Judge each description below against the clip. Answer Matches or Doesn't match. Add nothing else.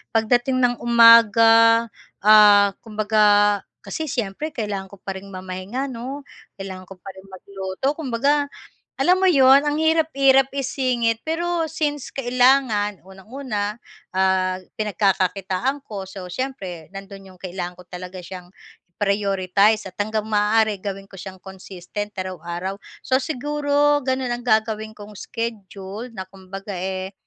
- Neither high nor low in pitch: Doesn't match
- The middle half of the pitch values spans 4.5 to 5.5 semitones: Matches